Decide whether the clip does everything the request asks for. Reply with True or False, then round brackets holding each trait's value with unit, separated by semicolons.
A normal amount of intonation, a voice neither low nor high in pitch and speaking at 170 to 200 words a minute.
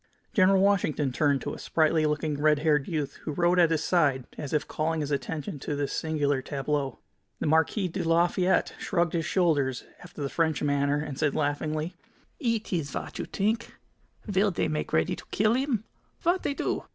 True (3.5 semitones; 155 Hz; 190 wpm)